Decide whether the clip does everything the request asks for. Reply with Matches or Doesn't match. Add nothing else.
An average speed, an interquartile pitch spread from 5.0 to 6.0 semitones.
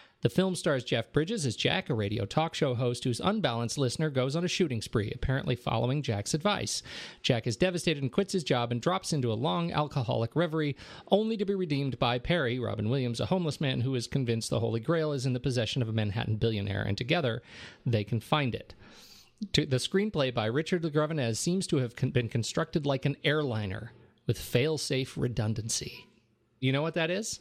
Matches